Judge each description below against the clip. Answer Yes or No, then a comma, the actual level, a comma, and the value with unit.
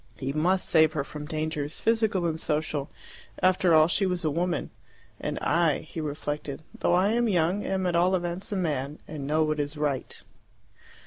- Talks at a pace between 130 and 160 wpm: No, average, 190 wpm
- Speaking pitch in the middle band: Yes, medium, 160 Hz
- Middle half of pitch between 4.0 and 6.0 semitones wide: No, average, 3.2 semitones